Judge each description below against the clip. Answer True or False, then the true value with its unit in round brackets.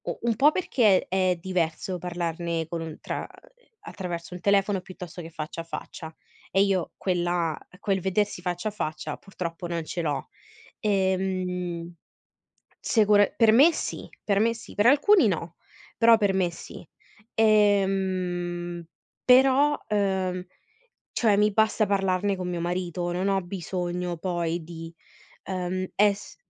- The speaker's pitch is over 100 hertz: True (185 Hz)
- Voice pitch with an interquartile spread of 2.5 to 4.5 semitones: True (2.8 semitones)